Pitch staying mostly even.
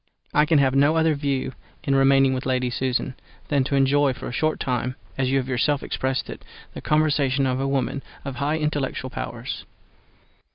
Yes: narrow, 1.8 semitones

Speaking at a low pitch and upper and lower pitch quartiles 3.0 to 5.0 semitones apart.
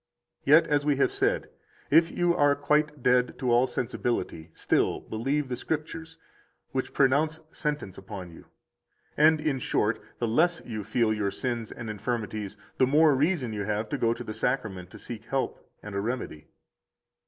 No: low, 125 Hz; wide, 5.6 semitones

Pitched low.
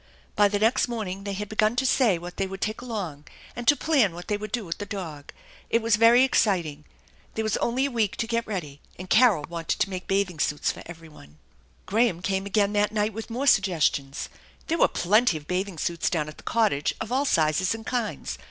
No: high, 205 Hz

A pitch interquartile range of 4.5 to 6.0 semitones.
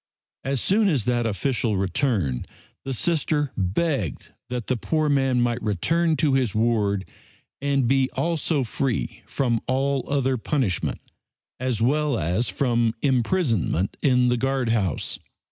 No: average, 3.8 semitones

